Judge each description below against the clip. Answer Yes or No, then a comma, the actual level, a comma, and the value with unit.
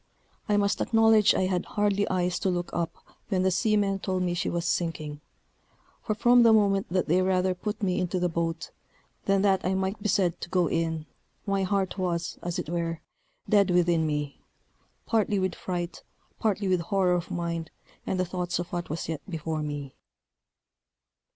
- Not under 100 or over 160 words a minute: No, average, 185 wpm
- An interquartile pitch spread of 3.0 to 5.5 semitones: No, narrow, 2.6 semitones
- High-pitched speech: No, medium, 180 Hz